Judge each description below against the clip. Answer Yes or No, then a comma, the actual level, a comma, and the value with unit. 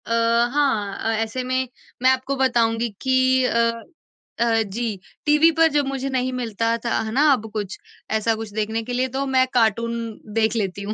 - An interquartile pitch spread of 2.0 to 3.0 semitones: Yes, average, 2.7 semitones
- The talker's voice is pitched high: Yes, high, 240 Hz